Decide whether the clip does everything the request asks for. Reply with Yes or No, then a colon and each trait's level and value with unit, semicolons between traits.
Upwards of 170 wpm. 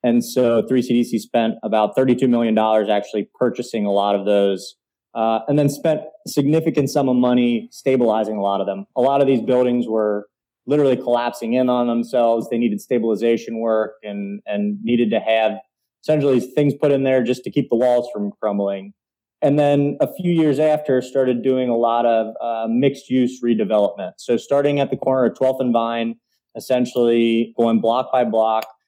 Yes: average, 180 wpm